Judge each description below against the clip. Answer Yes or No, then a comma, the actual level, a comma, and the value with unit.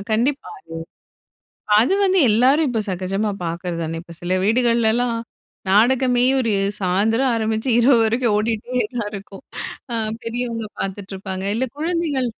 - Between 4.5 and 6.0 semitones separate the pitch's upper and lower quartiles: No, average, 4.0 semitones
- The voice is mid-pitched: No, high, 225 Hz